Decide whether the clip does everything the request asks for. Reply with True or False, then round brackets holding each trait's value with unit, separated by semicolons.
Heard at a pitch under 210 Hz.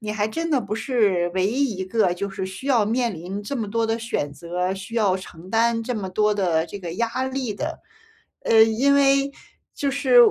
False (215 Hz)